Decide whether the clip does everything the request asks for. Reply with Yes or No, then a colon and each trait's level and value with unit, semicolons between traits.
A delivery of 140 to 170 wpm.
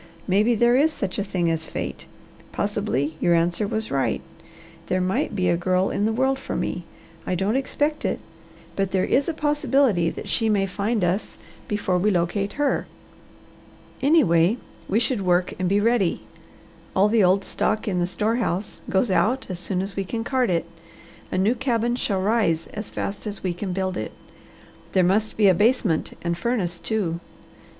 No: average, 185 wpm